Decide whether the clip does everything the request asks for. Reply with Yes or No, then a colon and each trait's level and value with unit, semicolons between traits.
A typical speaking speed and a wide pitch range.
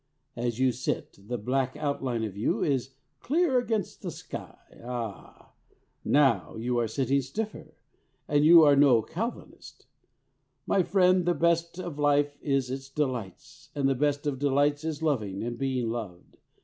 No: average, 155 wpm; average, 4.0 semitones